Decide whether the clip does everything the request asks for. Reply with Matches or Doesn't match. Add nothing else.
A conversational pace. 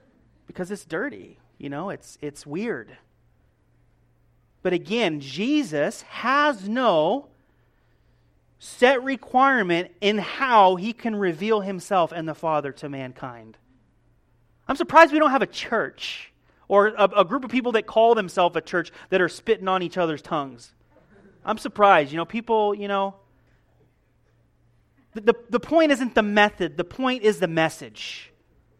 Matches